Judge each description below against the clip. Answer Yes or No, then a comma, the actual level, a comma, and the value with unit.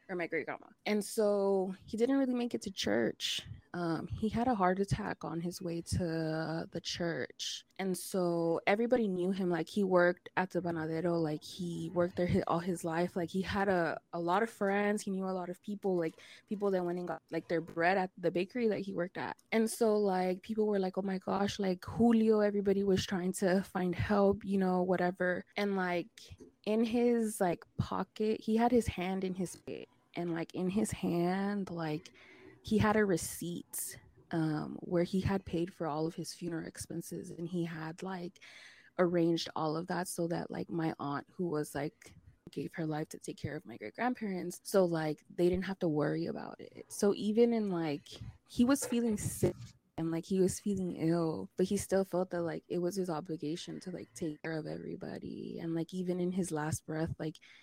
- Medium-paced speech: No, fast, 210 wpm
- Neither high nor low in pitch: Yes, medium, 180 Hz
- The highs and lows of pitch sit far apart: No, average, 3.2 semitones